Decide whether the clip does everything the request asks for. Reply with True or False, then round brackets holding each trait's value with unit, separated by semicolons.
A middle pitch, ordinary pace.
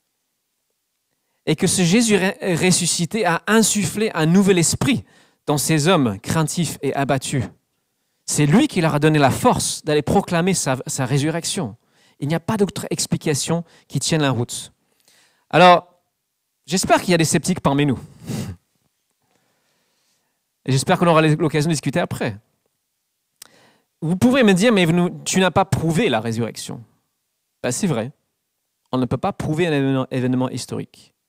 True (160 Hz; 155 wpm)